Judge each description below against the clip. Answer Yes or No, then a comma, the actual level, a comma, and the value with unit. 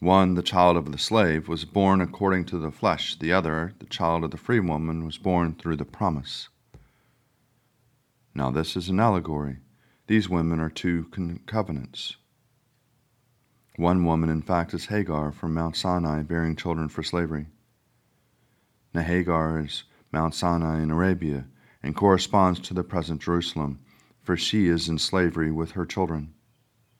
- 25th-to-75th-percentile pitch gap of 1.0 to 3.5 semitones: No, average, 4.1 semitones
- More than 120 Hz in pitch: No, very low, 85 Hz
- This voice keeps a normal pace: Yes, average, 155 wpm